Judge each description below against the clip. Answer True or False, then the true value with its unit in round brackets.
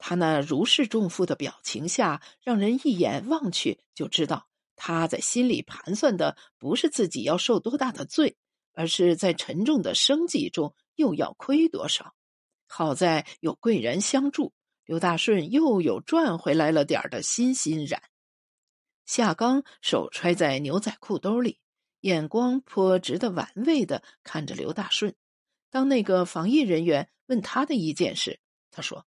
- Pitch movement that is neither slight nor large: False (7.3 semitones)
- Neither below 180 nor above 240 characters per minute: True (225 characters per minute)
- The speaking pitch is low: False (220 Hz)